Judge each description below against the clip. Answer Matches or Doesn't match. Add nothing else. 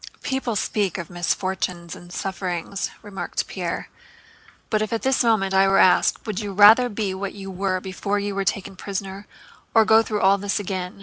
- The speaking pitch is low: Doesn't match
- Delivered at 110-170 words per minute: Doesn't match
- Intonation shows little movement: Matches